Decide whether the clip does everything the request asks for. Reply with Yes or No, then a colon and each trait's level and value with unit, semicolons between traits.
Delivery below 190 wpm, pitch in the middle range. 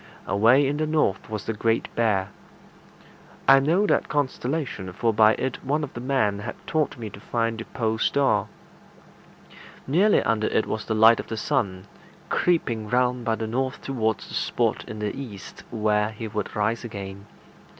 No: average, 175 wpm; low, 115 Hz